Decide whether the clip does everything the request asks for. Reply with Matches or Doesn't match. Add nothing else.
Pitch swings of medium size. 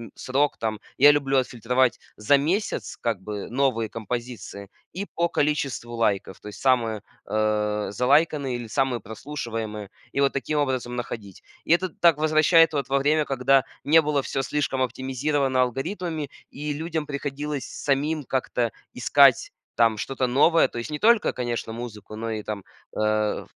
Matches